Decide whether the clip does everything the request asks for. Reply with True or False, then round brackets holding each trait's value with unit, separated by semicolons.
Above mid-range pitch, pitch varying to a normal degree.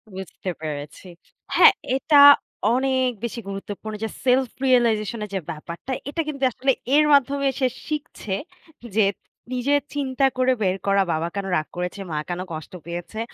False (225 Hz; 6.1 semitones)